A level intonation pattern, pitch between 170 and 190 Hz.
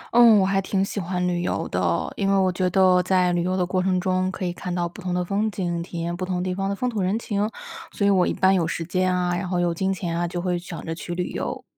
Yes: narrow, 1.5 semitones; medium, 185 Hz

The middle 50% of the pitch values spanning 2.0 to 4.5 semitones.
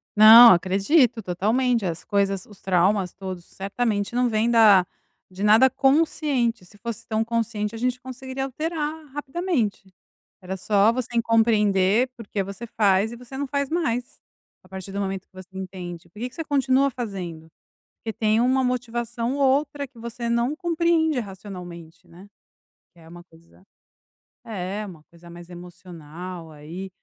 No: average, 4.9 semitones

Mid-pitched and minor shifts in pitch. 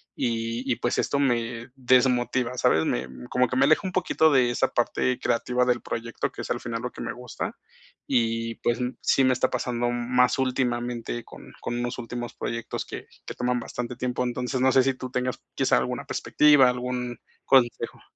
No: low, 125 Hz; narrow, 1.2 semitones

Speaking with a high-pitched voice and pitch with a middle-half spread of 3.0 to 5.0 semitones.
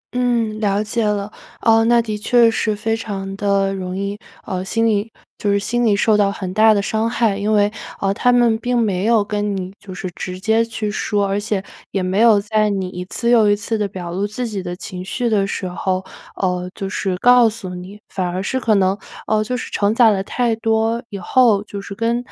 No: high, 210 Hz; narrow, 2.5 semitones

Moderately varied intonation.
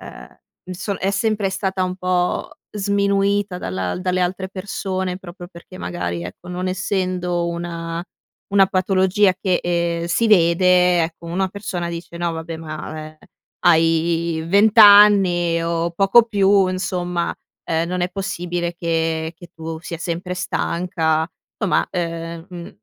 No: narrow, 2.2 semitones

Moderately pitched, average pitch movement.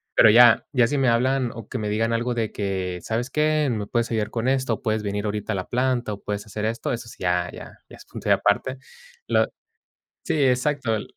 No: low, 115 Hz; average, 3.2 semitones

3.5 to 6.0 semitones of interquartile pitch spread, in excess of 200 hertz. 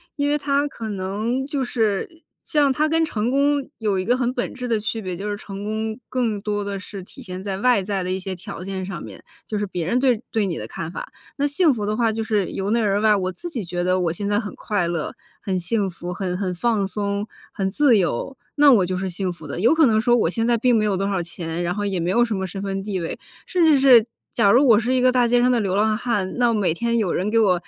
Yes: average, 4.3 semitones; high, 210 Hz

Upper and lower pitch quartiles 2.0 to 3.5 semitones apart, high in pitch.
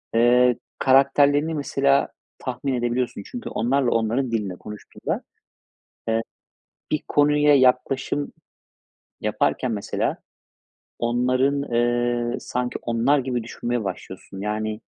No: average, 2.8 semitones; low, 125 Hz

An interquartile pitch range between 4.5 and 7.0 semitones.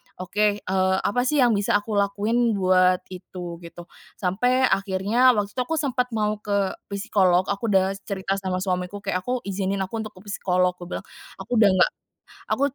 No: narrow, 2.6 semitones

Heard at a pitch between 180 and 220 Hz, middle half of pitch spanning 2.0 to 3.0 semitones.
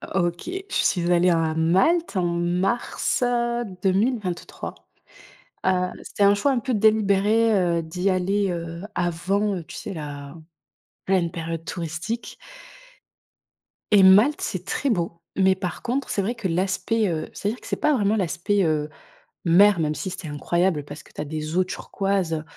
No: medium, 185 Hz; average, 3.4 semitones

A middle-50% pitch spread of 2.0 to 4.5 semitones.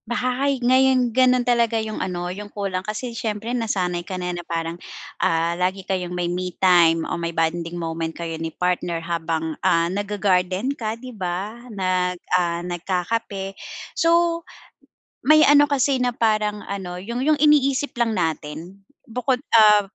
No: wide, 5.5 semitones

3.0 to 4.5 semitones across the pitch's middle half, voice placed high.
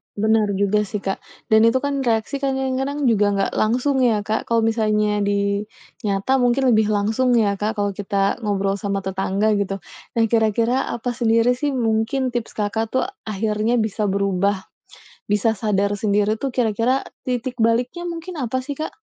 Yes: average, 3.4 semitones; high, 220 Hz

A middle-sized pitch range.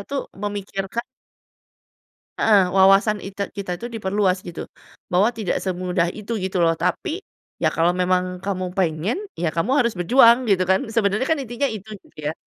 Yes: average, 3.3 semitones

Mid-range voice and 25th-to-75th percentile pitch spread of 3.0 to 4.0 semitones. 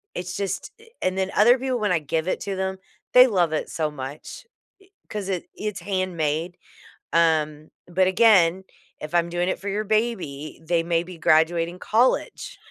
Yes: medium, 180 Hz; average, 3.4 semitones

